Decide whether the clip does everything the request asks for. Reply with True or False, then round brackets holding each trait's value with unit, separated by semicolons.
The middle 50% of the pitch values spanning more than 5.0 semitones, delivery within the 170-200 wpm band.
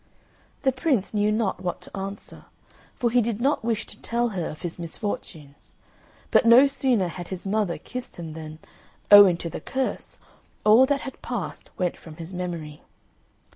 True (5.6 semitones; 175 wpm)